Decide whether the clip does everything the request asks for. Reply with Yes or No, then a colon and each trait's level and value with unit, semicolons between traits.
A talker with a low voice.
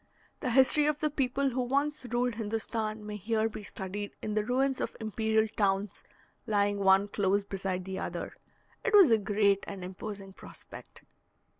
No: high, 215 Hz